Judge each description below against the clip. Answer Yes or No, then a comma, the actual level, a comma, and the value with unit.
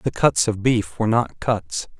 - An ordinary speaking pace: No, fast, 210 wpm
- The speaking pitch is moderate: No, low, 110 Hz